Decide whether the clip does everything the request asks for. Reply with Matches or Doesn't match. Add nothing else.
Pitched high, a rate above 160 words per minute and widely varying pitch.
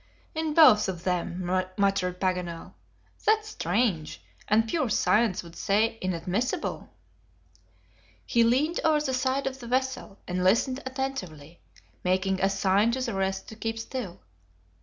Doesn't match